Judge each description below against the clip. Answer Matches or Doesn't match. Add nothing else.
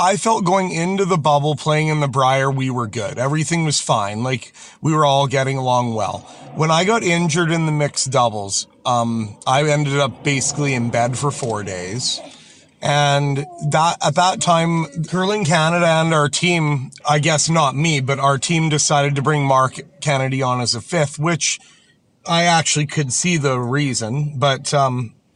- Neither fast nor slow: Matches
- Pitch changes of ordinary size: Matches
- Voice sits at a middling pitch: Matches